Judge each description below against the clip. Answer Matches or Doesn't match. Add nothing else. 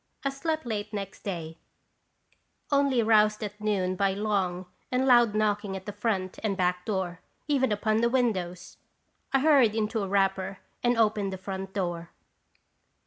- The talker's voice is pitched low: Doesn't match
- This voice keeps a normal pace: Matches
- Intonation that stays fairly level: Doesn't match